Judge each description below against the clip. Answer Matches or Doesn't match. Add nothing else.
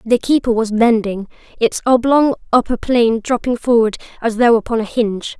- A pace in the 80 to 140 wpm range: Doesn't match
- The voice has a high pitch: Matches